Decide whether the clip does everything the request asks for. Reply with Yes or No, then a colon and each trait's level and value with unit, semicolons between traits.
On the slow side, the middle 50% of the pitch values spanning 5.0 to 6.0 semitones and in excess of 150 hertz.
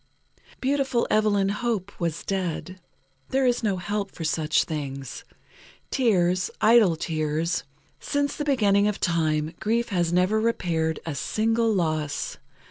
Yes: slow, 125 wpm; wide, 5.5 semitones; high, 190 Hz